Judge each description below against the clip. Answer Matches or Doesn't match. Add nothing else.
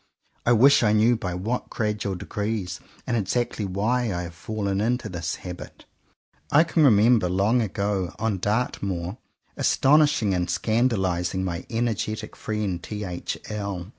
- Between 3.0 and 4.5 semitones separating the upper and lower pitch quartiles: Matches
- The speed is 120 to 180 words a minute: Matches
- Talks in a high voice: Doesn't match